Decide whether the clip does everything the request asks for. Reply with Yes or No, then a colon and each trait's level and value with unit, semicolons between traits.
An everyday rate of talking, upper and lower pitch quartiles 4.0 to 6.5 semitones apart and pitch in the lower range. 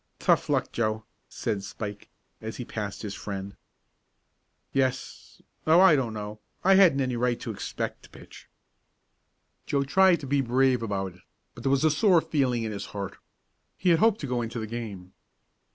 Yes: average, 180 wpm; average, 5.0 semitones; low, 120 Hz